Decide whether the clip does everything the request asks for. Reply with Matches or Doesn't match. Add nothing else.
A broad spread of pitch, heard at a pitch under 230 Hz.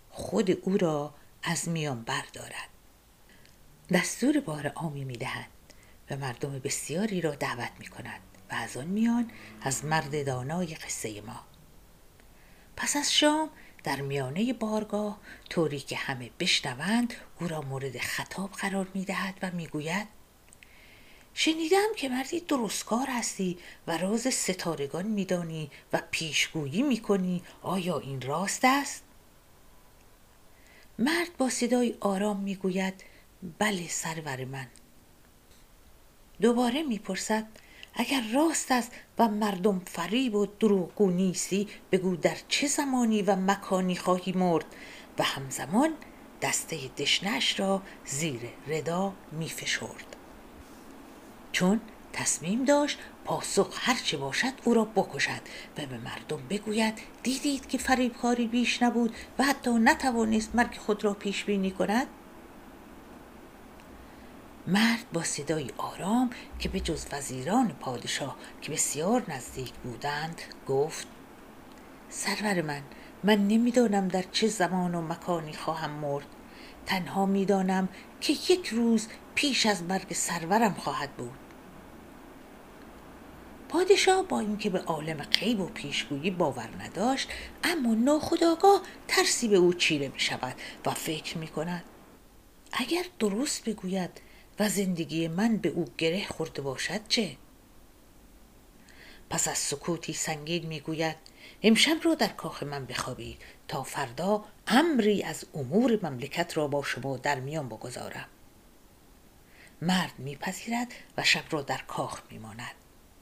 Matches